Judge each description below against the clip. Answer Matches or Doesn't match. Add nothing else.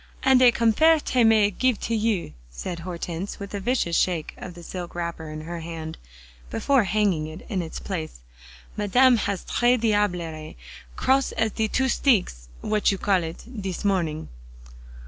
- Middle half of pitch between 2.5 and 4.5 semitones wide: Doesn't match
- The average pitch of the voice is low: Doesn't match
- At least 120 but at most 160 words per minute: Doesn't match